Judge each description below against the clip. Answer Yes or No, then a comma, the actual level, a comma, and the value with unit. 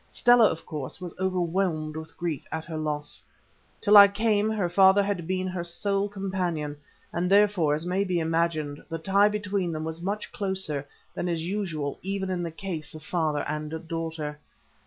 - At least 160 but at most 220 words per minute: Yes, average, 180 wpm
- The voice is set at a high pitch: No, medium, 175 Hz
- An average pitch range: Yes, average, 3.7 semitones